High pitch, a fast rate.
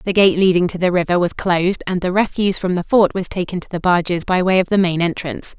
No: medium, 180 Hz; fast, 270 wpm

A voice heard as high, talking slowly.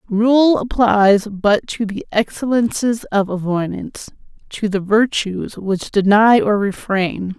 Yes: high, 210 Hz; slow, 115 wpm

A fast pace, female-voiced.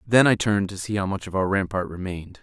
No: fast, 275 wpm; male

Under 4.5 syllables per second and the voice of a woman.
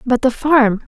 Yes: 3.9 syllables/s; female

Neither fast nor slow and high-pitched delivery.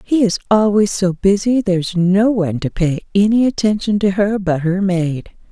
Yes: average, 185 wpm; high, 195 Hz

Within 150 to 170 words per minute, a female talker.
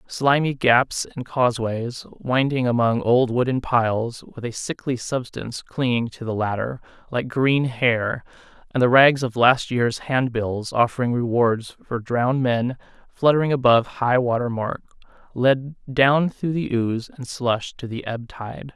No: average, 155 wpm; male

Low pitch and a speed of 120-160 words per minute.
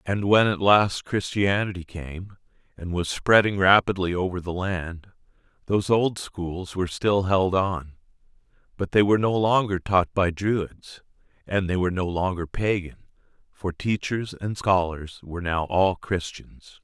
Yes: very low, 95 Hz; average, 150 wpm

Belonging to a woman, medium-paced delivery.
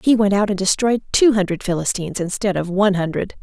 No: female; fast, 210 wpm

